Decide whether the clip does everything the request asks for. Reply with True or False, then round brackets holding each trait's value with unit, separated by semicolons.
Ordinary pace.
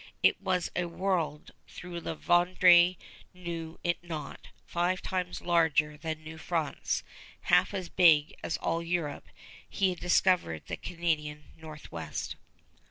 False (130 wpm)